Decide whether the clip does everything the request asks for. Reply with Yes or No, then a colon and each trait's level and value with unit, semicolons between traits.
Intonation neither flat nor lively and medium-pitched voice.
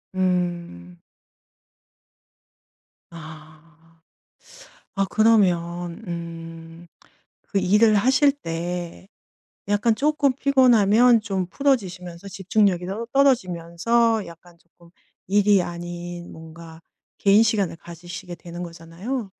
Yes: average, 4.2 semitones; medium, 180 Hz